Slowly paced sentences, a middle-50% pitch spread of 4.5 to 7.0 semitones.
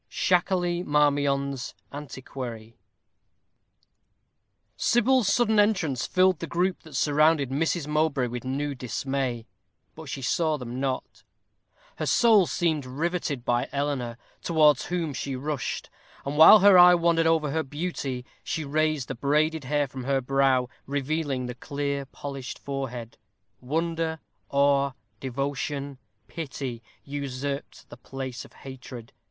No: slow, 125 wpm; average, 3.5 semitones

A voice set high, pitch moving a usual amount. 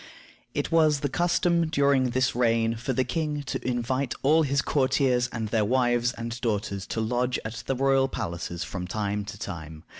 No: low, 125 Hz; average, 3.6 semitones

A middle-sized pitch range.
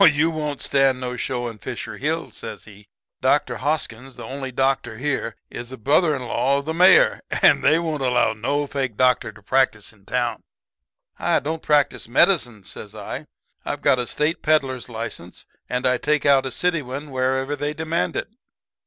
Yes: average, 3.4 semitones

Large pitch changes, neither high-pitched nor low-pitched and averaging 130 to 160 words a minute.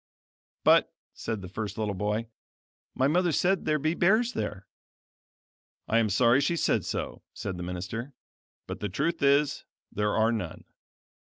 No: wide, 6.7 semitones; low, 115 Hz; average, 155 wpm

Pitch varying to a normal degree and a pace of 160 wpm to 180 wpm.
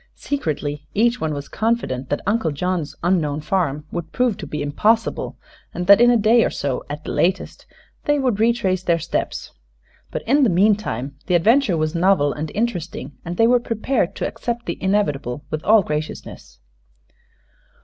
No: wide, 7.0 semitones; average, 170 wpm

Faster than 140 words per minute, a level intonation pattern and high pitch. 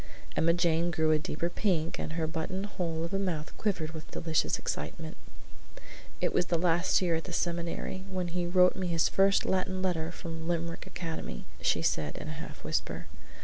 No: average, 185 wpm; narrow, 2.1 semitones; medium, 170 Hz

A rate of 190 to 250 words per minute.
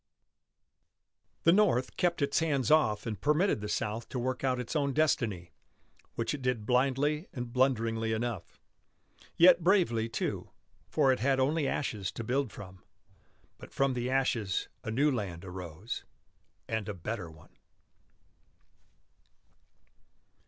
No: slow, 135 wpm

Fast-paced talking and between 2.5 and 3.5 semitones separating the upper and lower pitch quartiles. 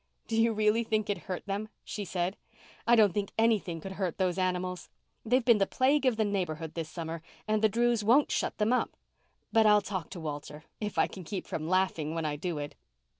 No: fast, 215 wpm; average, 4.0 semitones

